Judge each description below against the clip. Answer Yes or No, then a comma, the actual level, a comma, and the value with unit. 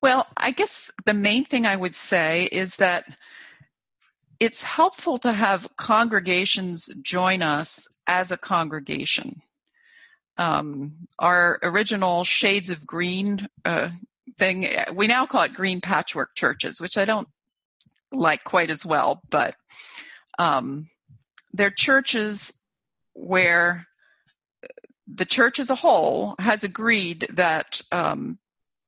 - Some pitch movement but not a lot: Yes, average, 5.0 semitones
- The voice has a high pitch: Yes, high, 195 Hz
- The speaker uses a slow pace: Yes, slow, 120 wpm